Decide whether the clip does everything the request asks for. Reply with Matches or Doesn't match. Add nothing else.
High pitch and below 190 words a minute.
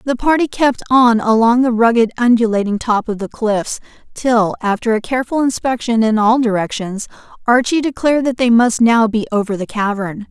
Matches